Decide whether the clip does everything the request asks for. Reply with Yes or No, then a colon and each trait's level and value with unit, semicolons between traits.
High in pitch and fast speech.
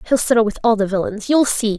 Yes: high, 220 Hz; fast, 270 wpm